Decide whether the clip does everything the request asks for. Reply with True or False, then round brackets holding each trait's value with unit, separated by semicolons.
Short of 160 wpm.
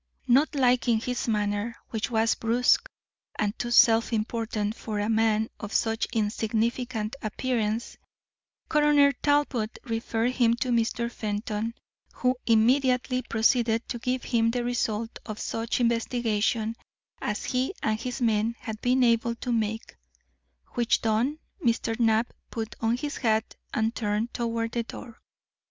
True (140 wpm)